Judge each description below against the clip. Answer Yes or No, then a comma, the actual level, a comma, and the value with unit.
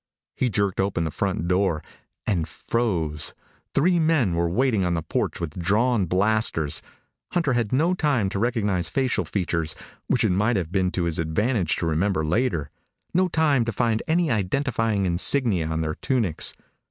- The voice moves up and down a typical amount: No, wide, 6.5 semitones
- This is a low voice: Yes, low, 100 Hz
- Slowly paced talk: No, average, 165 wpm